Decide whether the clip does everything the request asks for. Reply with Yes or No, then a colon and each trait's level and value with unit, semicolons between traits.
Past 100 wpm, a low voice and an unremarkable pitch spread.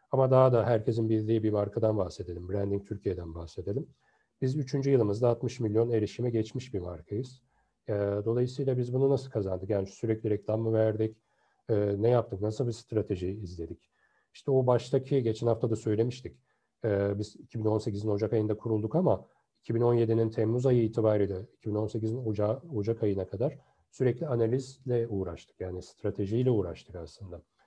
Yes: fast, 140 wpm; low, 110 Hz; average, 3.1 semitones